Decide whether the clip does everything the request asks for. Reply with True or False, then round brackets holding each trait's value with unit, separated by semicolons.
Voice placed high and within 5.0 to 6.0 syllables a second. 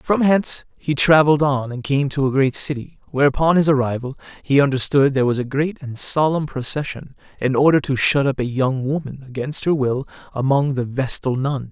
False (140 Hz; 5.5 syllables/s)